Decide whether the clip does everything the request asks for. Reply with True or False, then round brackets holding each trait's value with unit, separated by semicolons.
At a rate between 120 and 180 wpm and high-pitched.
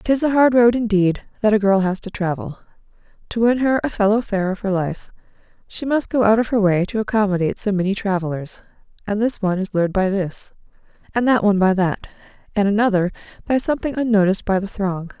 False (200 wpm; 205 Hz)